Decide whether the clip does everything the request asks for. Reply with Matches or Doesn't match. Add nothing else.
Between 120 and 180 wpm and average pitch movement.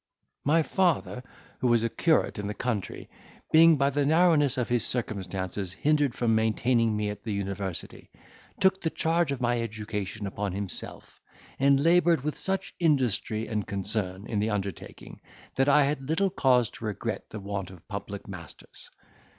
Doesn't match